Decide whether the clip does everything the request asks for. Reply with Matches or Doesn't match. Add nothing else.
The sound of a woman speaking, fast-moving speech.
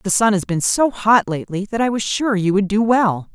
Matches